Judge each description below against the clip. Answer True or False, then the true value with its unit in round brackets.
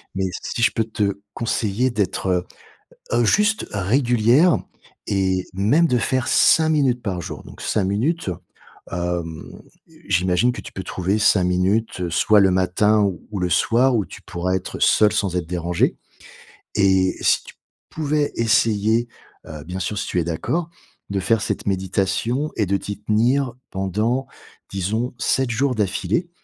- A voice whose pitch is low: True (105 Hz)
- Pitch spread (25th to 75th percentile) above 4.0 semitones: True (4.5 semitones)